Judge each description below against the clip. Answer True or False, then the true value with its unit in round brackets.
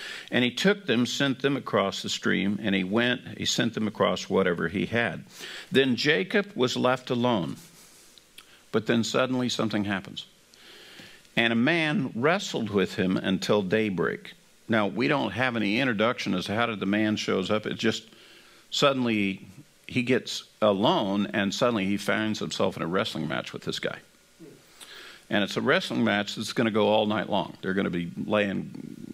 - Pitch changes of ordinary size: True (3.5 semitones)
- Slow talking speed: False (175 wpm)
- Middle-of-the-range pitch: False (115 Hz)